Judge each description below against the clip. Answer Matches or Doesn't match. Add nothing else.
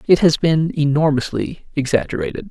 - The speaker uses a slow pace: Matches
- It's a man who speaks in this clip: Matches